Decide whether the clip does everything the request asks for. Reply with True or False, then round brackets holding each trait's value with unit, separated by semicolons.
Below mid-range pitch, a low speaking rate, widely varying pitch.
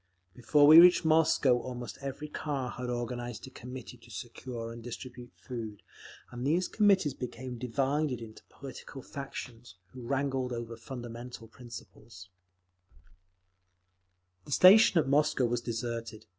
False (125 Hz; 130 wpm; 2.9 semitones)